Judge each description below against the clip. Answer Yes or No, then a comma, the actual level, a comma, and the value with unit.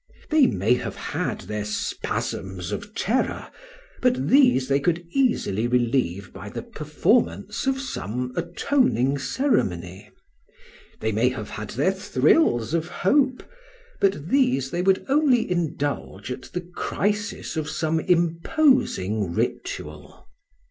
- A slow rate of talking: Yes, slow, 120 wpm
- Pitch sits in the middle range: Yes, medium, 155 Hz